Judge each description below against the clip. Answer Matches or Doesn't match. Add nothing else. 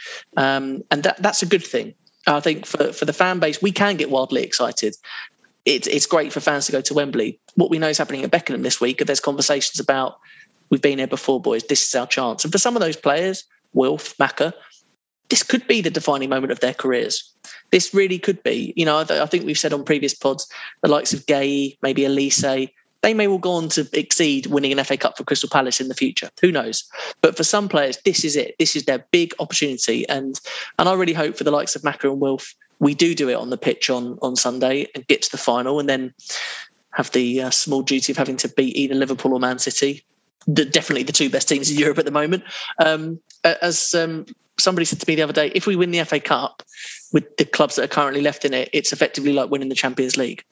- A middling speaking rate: Doesn't match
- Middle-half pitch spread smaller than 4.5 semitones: Matches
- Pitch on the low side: Doesn't match